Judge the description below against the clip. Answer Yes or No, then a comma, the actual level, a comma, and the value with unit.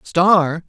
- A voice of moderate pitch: Yes, medium, 175 Hz